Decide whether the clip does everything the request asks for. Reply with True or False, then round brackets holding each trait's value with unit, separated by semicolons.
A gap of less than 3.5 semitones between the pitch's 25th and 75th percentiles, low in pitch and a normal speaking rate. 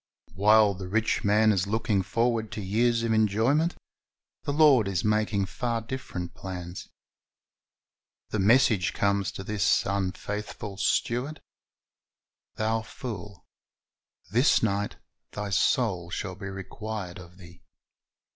False (2.8 semitones; 105 Hz; 120 wpm)